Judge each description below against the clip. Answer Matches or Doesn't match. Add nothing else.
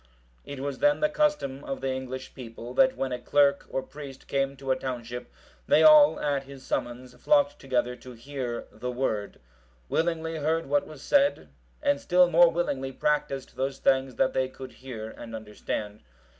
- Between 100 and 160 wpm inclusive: Doesn't match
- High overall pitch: Doesn't match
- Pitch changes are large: Doesn't match